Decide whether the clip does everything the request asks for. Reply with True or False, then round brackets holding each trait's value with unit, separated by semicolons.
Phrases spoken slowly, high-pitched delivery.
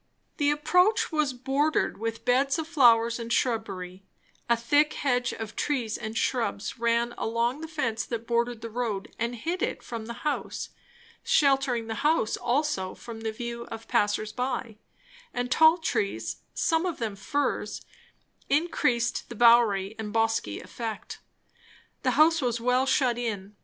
False (150 wpm; 235 Hz)